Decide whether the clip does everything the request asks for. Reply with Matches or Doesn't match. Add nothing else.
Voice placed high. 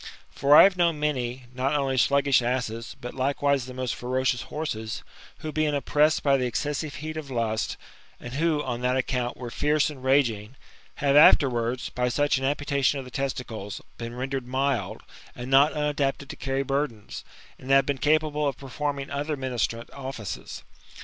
Doesn't match